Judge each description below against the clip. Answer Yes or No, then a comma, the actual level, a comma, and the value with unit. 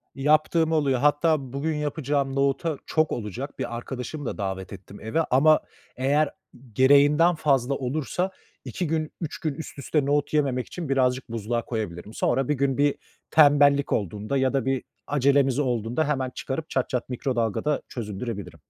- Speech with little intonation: No, average, 3.2 semitones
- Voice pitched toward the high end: No, low, 135 Hz